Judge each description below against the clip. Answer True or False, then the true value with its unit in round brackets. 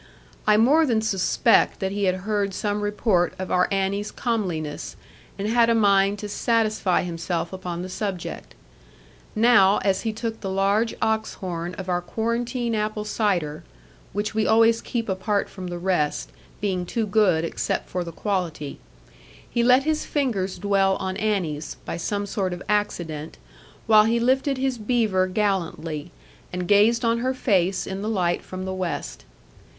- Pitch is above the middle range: True (200 Hz)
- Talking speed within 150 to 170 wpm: True (165 wpm)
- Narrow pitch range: False (3.3 semitones)